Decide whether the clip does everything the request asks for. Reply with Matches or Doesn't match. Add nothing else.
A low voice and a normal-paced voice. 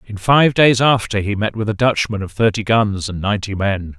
Doesn't match